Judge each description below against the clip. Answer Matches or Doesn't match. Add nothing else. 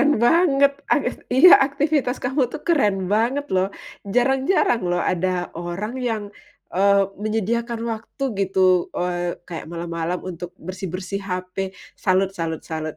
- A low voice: Doesn't match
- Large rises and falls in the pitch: Matches